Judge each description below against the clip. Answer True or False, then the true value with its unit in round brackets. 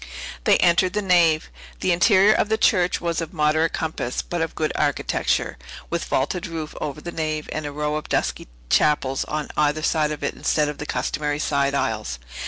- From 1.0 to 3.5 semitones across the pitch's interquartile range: True (2.5 semitones)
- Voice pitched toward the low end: False (155 Hz)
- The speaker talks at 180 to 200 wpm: True (195 wpm)